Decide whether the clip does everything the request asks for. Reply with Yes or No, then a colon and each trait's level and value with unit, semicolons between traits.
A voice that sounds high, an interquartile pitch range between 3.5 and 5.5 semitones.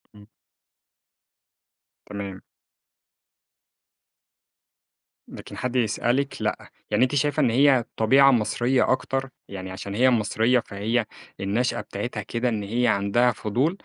No: low, 120 Hz; average, 3.8 semitones